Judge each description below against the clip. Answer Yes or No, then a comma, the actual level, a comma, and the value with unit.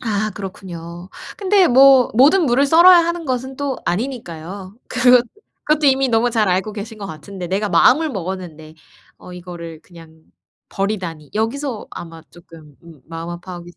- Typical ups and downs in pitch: No, wide, 7.2 semitones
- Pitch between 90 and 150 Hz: No, high, 200 Hz